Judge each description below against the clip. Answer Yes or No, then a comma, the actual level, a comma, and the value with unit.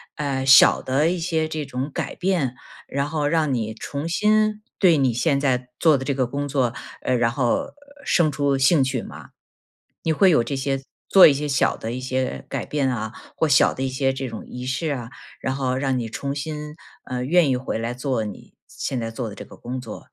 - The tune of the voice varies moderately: Yes, average, 3.0 semitones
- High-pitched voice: No, low, 135 Hz